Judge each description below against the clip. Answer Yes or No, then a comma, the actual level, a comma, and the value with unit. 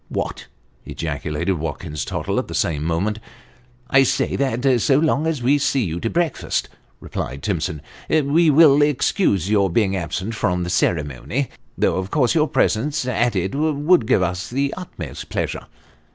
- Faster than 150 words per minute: Yes, average, 175 wpm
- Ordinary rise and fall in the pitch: No, wide, 8.1 semitones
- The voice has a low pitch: Yes, low, 115 Hz